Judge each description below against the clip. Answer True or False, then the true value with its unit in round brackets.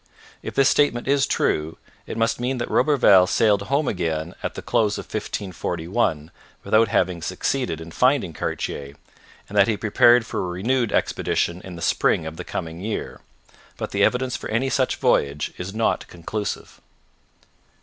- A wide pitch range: True (6.1 semitones)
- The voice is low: True (105 Hz)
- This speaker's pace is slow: False (165 wpm)